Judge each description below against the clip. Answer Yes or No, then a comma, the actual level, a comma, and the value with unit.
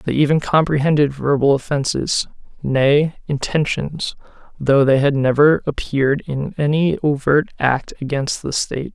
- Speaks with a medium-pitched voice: Yes, medium, 145 Hz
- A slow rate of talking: Yes, slow, 125 wpm